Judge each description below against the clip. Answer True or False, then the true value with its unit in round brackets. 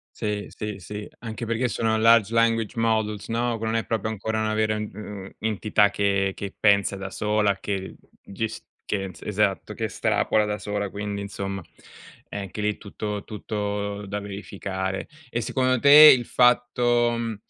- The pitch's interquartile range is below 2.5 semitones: True (1.9 semitones)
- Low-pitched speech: True (105 Hz)